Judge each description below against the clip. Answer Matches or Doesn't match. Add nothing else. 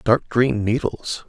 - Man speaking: Matches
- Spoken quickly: Doesn't match